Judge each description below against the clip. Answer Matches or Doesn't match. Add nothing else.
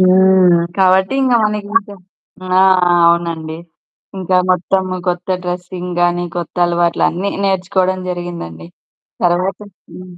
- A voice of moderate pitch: Matches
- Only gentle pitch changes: Matches